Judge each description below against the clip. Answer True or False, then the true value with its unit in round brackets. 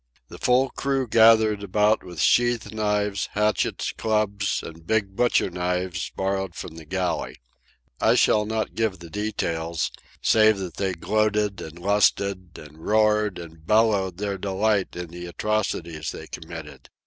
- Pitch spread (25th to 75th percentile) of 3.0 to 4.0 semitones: True (3.3 semitones)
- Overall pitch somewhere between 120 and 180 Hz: False (100 Hz)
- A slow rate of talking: False (145 wpm)